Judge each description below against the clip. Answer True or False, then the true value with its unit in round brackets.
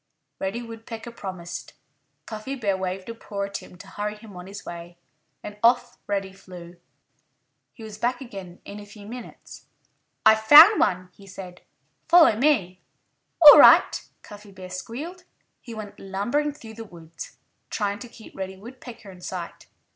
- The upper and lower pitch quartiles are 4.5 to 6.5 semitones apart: False (3.7 semitones)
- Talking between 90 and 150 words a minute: False (160 wpm)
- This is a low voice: False (205 Hz)